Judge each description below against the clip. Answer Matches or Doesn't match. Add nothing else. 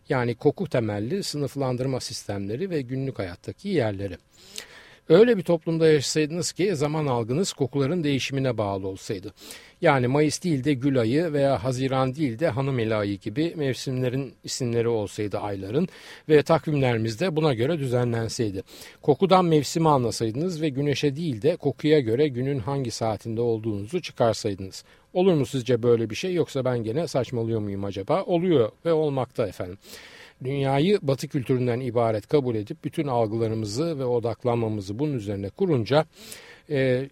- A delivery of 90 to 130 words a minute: Doesn't match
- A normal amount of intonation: Matches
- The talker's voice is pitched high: Doesn't match